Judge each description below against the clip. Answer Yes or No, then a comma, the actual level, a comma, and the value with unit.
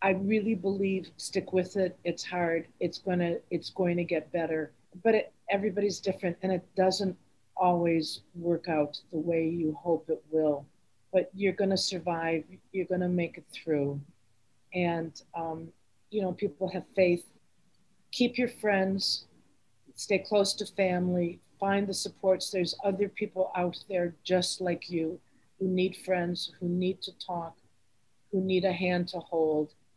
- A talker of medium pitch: Yes, medium, 180 Hz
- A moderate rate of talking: Yes, average, 160 wpm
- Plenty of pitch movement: No, narrow, 2.6 semitones